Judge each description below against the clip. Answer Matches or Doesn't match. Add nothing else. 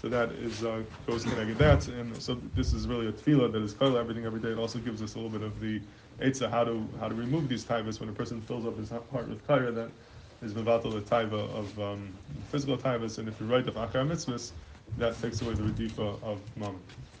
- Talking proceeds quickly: Matches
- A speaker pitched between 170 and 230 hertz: Doesn't match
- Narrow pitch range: Matches